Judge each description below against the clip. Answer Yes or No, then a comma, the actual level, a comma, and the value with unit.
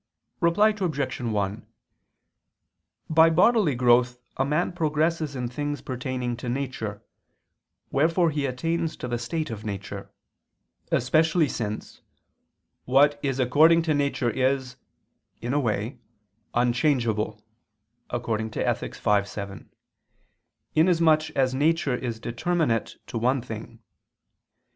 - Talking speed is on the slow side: Yes, slow, 110 wpm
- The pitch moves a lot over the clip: No, average, 4.8 semitones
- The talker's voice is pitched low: Yes, low, 130 Hz